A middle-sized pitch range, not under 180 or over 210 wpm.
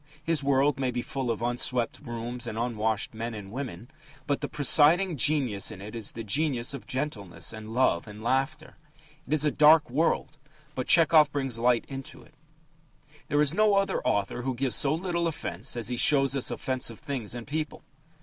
Yes: average, 4.3 semitones; average, 190 wpm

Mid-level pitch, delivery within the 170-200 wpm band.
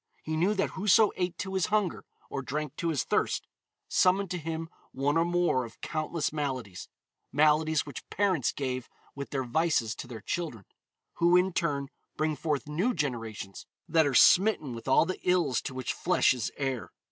Yes: medium, 155 Hz; average, 180 wpm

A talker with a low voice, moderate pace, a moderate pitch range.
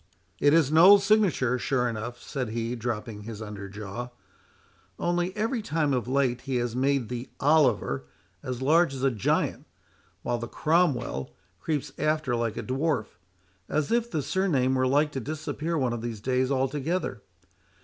Yes: low, 130 Hz; average, 160 wpm; average, 4.5 semitones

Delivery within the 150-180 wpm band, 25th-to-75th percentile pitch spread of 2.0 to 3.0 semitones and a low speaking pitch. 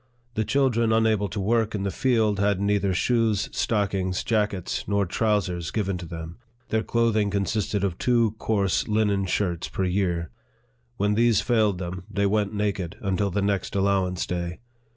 Yes: average, 160 wpm; narrow, 2.6 semitones; low, 100 Hz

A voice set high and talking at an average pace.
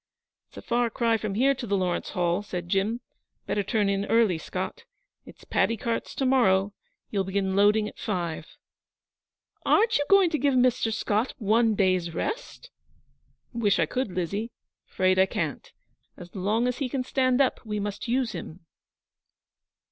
Yes: high, 215 Hz; average, 165 wpm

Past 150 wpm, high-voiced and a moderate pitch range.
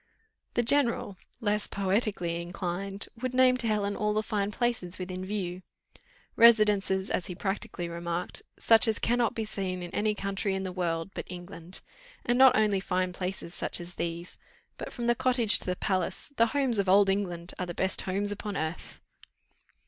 Yes: average, 180 wpm; high, 195 Hz; average, 3.2 semitones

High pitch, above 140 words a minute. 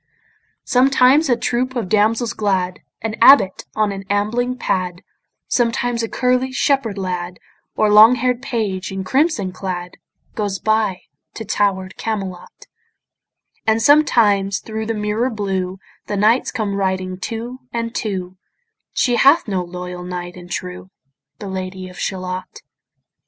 No: high, 210 Hz; slow, 135 wpm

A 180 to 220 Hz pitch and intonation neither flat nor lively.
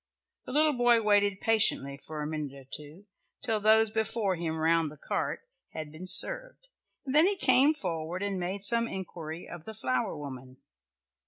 No: high, 190 Hz; wide, 6.5 semitones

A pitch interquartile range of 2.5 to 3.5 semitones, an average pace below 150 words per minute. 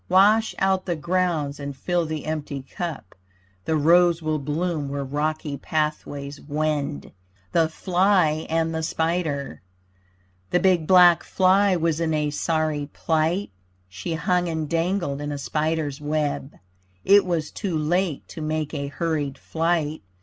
Yes: average, 2.9 semitones; average, 140 wpm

